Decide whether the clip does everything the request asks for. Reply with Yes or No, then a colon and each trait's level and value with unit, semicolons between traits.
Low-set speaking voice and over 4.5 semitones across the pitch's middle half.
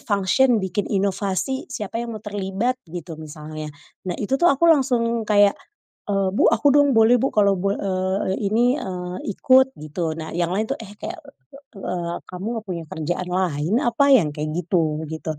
No: high, 195 Hz; average, 4.9 semitones